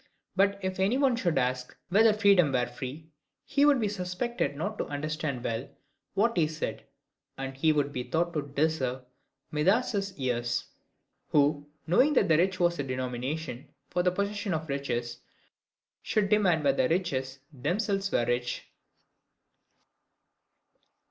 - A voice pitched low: No, medium, 160 Hz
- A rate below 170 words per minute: Yes, average, 140 wpm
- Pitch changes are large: Yes, wide, 6.7 semitones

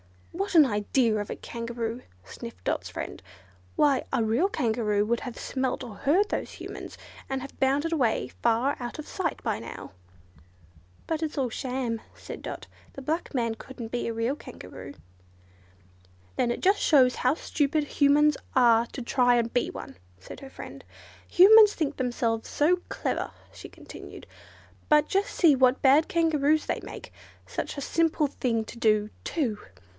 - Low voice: No, very high, 260 Hz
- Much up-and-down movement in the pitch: No, average, 4.6 semitones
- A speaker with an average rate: Yes, average, 160 wpm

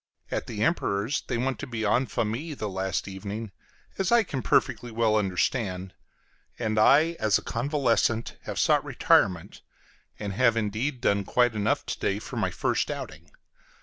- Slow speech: No, average, 165 wpm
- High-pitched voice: No, low, 110 Hz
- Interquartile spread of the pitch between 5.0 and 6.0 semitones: No, average, 4.0 semitones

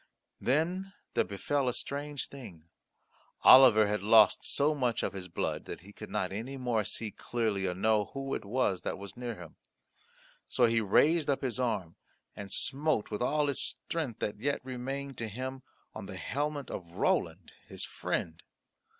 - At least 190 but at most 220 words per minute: No, average, 175 wpm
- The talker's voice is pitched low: Yes, low, 120 Hz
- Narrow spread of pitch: No, average, 5.1 semitones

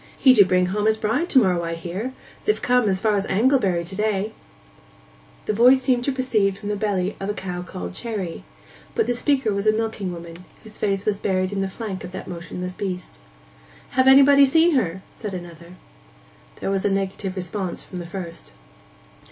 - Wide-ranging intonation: No, average, 3.7 semitones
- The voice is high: Yes, high, 200 Hz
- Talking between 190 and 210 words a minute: Yes, average, 195 wpm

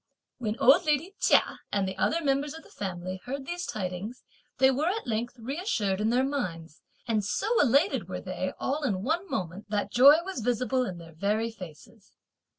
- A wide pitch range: Yes, wide, 6.2 semitones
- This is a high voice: Yes, high, 240 Hz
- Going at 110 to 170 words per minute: No, average, 185 wpm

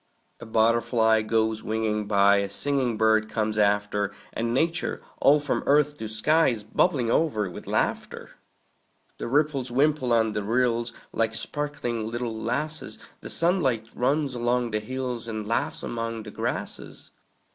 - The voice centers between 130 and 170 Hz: No, low, 115 Hz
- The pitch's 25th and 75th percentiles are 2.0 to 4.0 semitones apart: Yes, average, 3.5 semitones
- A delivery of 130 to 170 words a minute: Yes, average, 145 wpm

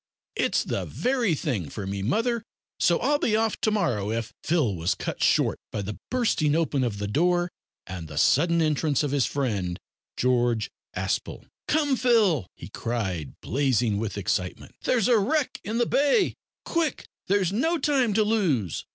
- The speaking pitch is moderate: Yes, medium, 155 Hz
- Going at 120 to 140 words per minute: No, average, 170 wpm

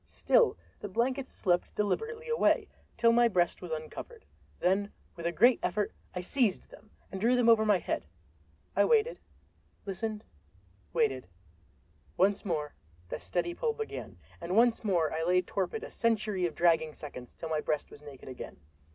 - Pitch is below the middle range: No, high, 195 Hz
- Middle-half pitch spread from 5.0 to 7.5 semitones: Yes, wide, 5.6 semitones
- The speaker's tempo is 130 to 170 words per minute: Yes, average, 165 wpm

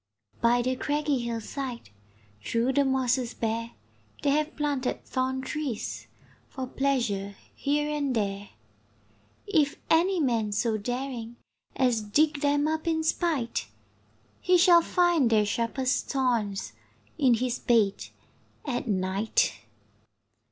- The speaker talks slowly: Yes, slow, 120 wpm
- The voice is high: Yes, very high, 255 Hz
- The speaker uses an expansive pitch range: No, average, 4.2 semitones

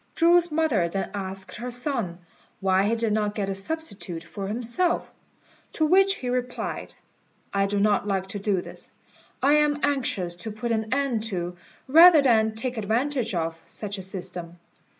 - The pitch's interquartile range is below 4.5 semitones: No, wide, 5.6 semitones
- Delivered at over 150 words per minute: Yes, average, 170 wpm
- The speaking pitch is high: Yes, high, 220 Hz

